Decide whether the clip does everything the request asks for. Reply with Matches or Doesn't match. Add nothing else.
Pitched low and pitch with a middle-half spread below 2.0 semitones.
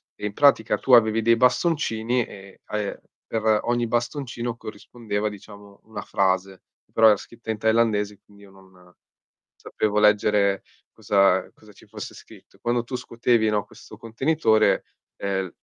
Doesn't match